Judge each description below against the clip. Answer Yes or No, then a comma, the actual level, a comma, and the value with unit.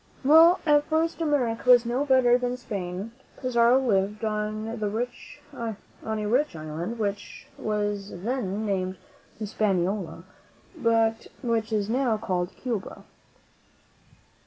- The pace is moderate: No, slow, 110 wpm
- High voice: Yes, high, 225 Hz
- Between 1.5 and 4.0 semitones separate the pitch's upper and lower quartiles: Yes, average, 3.5 semitones